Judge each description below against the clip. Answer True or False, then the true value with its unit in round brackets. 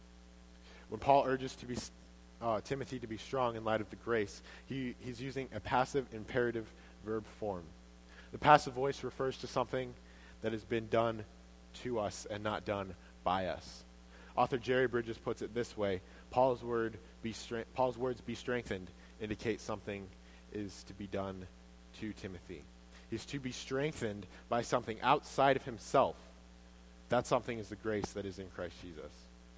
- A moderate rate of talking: True (165 wpm)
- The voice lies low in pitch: True (105 Hz)